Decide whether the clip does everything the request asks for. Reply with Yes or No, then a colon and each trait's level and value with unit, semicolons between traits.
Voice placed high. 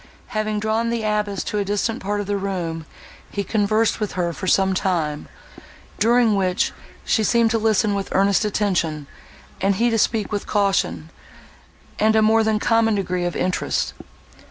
Yes: high, 205 Hz